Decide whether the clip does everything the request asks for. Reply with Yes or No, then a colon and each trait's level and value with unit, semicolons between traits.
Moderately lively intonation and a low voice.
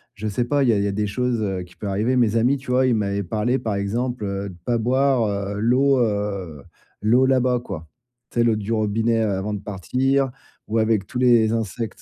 Yes: average, 3.6 semitones; low, 110 Hz